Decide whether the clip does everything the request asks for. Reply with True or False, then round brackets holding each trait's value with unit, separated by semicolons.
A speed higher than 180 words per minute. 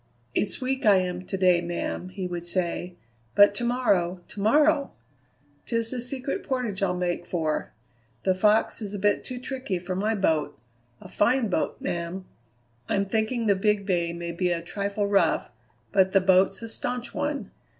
False (175 wpm)